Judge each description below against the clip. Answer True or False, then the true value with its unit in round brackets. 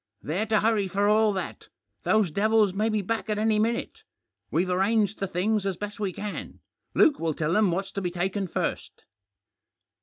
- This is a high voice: True (205 Hz)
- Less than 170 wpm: False (185 wpm)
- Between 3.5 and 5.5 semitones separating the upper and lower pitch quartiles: False (2.5 semitones)